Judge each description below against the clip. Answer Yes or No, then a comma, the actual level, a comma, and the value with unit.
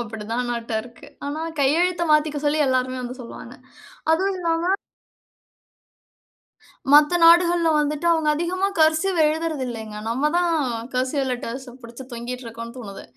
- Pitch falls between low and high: No, very high, 285 Hz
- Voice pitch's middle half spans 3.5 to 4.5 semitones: No, wide, 5.4 semitones